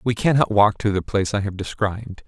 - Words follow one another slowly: No, fast, 235 wpm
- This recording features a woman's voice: No, male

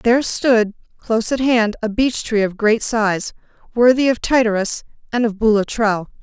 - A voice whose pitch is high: Yes, high, 225 Hz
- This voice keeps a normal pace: Yes, average, 165 wpm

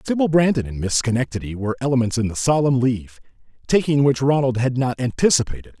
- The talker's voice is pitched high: No, low, 130 Hz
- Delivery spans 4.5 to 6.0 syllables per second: No, 6.5 syllables/s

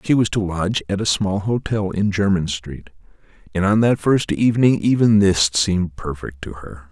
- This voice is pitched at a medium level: No, very low, 95 Hz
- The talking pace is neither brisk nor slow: Yes, average, 190 wpm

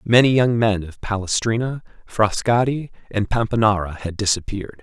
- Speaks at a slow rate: Yes, slow, 125 wpm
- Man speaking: Yes, male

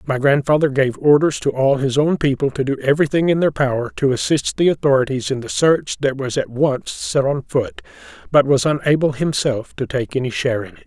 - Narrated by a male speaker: Yes, male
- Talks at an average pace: No, fast, 215 wpm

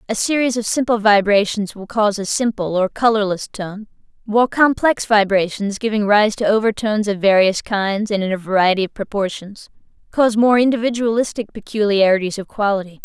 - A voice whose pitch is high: Yes, high, 210 Hz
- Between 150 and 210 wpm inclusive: Yes, average, 155 wpm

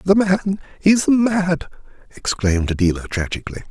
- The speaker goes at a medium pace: No, slow, 115 wpm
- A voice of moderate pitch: Yes, medium, 160 Hz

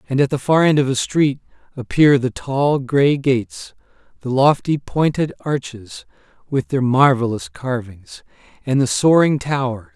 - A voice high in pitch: No, low, 135 Hz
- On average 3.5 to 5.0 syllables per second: Yes, 4.4 syllables/s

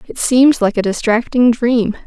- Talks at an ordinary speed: Yes, average, 175 wpm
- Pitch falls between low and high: No, high, 235 Hz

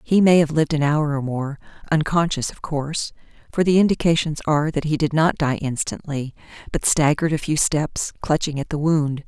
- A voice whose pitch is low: No, medium, 150 Hz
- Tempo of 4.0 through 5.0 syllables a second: No, 5.4 syllables/s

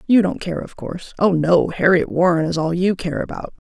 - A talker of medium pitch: Yes, medium, 170 Hz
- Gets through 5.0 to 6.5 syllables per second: Yes, 5.5 syllables/s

